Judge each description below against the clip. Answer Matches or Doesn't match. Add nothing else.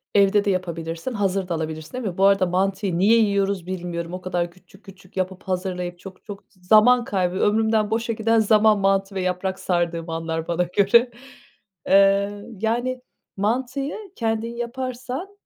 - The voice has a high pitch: Matches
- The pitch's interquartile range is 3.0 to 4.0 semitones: Matches